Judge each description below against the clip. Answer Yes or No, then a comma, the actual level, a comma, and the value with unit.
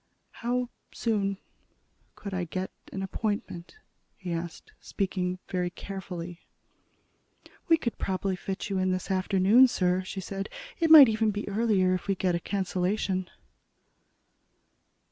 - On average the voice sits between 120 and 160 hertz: No, high, 190 Hz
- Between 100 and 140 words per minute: Yes, slow, 135 wpm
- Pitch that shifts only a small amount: Yes, narrow, 2.2 semitones